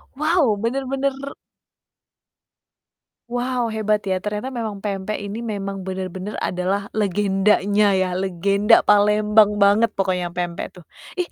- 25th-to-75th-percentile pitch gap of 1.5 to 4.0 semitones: Yes, narrow, 2.5 semitones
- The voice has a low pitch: No, high, 205 Hz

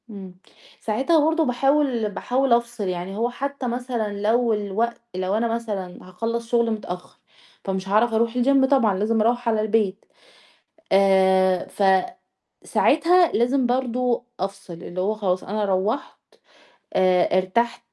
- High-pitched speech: Yes, high, 225 Hz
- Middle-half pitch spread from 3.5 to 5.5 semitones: Yes, average, 4.0 semitones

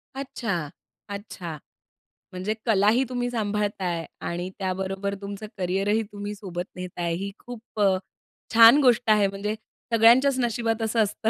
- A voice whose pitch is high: Yes, high, 205 Hz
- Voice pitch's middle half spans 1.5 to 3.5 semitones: Yes, average, 3.0 semitones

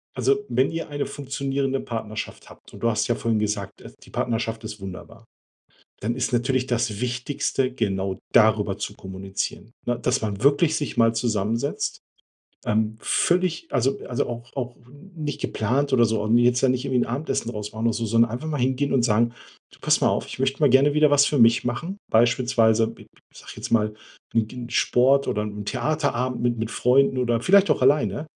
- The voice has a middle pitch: No, low, 120 Hz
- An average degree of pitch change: Yes, average, 3.3 semitones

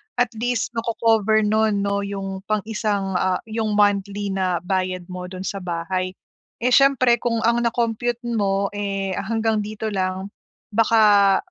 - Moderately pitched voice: No, high, 205 Hz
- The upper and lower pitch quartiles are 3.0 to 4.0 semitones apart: No, narrow, 2.6 semitones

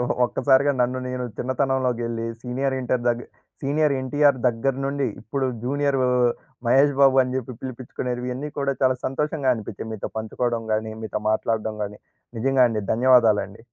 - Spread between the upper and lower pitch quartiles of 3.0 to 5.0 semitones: No, narrow, 2.6 semitones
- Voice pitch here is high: No, low, 125 Hz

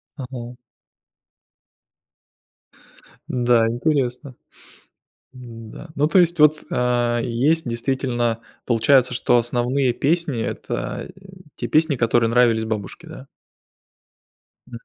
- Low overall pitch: Yes, low, 125 Hz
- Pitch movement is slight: No, average, 3.1 semitones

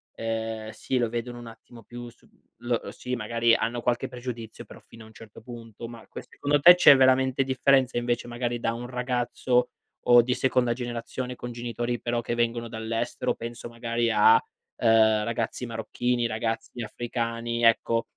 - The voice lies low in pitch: Yes, low, 120 Hz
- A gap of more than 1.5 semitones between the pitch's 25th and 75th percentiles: No, narrow, 1.2 semitones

